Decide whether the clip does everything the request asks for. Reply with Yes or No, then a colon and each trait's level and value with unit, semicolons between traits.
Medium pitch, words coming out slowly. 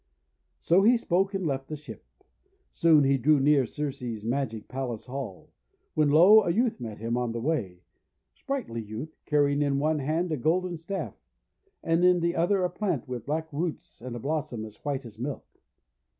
No: medium, 145 Hz; average, 190 wpm